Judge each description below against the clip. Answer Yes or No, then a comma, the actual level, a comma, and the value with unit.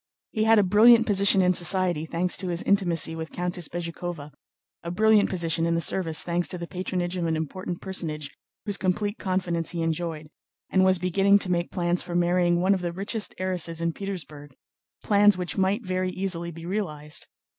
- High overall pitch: No, medium, 180 Hz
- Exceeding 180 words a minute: Yes, average, 190 wpm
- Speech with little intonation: Yes, narrow, 2.3 semitones